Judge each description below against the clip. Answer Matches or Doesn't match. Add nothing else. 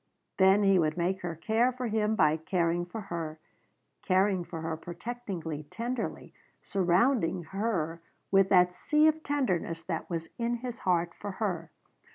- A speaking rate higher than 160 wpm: Doesn't match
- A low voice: Doesn't match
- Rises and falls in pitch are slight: Doesn't match